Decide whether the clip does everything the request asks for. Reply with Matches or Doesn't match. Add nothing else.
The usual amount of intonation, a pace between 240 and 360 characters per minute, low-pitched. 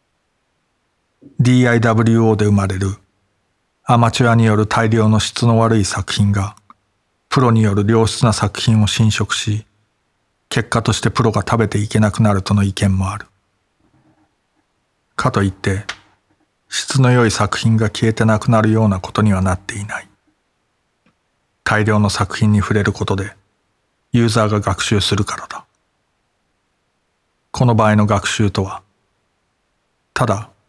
Doesn't match